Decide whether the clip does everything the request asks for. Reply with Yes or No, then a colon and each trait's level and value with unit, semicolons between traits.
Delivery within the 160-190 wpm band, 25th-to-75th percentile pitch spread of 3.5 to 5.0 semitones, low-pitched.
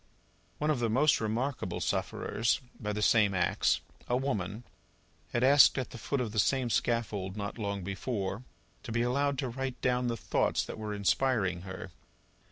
Yes: average, 175 wpm; average, 4.0 semitones; low, 115 Hz